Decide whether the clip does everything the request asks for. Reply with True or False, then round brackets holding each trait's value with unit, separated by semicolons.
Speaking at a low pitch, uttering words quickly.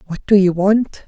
False (195 Hz; 225 wpm)